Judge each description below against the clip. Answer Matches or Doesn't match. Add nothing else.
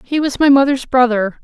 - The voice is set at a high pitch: Matches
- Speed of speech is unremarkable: Doesn't match